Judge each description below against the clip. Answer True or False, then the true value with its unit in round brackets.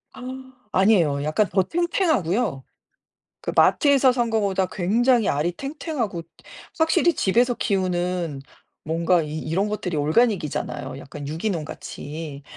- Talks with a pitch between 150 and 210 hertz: True (185 Hz)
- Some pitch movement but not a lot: False (7.2 semitones)